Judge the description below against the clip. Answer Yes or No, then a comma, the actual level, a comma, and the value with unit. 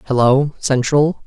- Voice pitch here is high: No, low, 135 Hz